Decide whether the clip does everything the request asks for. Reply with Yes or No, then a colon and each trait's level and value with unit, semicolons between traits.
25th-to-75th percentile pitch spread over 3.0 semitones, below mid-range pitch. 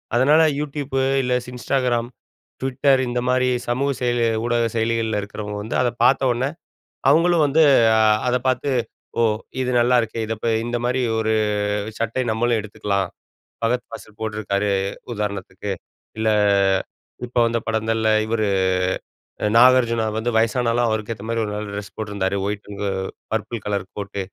No: average, 2.7 semitones; low, 115 Hz